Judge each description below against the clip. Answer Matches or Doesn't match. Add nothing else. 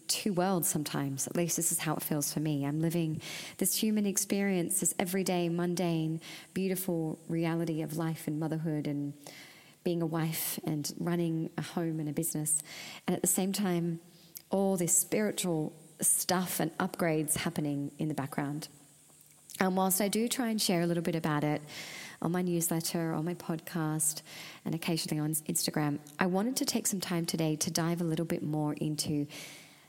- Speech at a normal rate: Matches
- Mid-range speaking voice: Matches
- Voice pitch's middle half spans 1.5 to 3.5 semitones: Matches